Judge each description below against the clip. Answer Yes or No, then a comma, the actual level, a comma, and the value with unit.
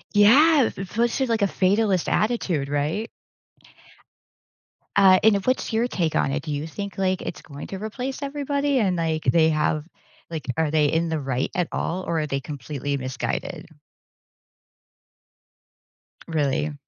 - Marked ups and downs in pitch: Yes, wide, 6.4 semitones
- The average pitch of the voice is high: No, medium, 175 Hz